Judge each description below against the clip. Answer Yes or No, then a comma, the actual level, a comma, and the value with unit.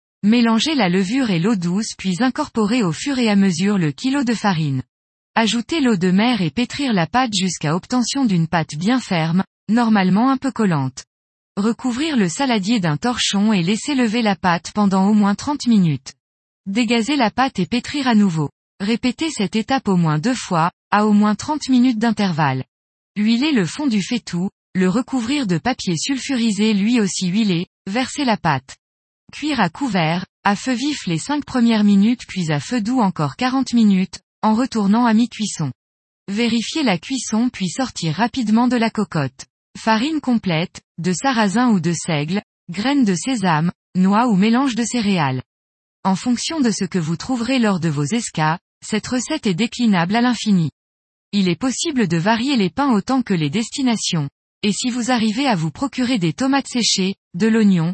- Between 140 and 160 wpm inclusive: No, average, 175 wpm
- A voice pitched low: No, high, 215 Hz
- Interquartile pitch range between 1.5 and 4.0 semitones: No, average, 5.3 semitones